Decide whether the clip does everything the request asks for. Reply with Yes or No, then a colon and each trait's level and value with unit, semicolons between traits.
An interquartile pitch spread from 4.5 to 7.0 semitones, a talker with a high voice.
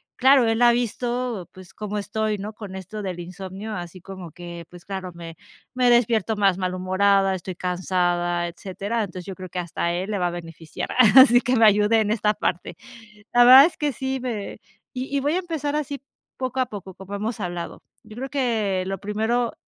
Yes: average, 4.8 semitones; high, 205 Hz